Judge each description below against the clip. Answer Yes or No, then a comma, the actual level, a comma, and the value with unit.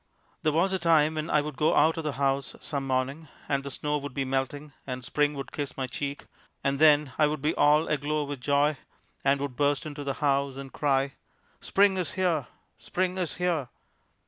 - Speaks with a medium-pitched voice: Yes, medium, 145 Hz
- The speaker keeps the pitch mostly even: Yes, narrow, 1.9 semitones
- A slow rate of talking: No, fast, 205 wpm